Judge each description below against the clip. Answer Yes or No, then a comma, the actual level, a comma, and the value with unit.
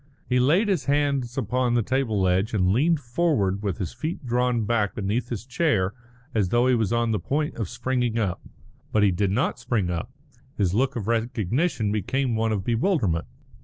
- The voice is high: No, low, 115 Hz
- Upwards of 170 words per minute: Yes, average, 190 wpm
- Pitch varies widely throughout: No, average, 4.1 semitones